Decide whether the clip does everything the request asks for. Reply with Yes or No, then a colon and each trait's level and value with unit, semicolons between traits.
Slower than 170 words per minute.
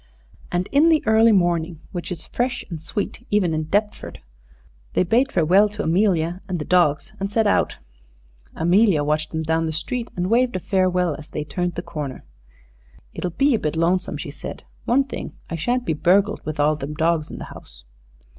No: average, 195 wpm